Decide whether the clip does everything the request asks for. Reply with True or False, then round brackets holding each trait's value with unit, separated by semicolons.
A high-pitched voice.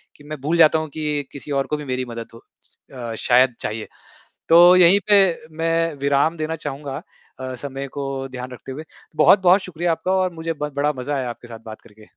False (145 Hz)